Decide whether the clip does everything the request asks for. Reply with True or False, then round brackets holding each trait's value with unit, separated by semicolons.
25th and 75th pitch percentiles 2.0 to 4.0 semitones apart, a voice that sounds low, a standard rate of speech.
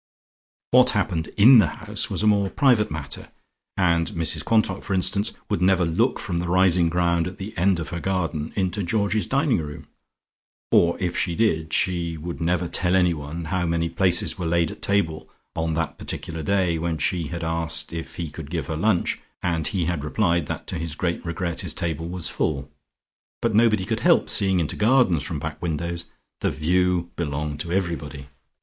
True (2.5 semitones; 85 Hz; 190 wpm)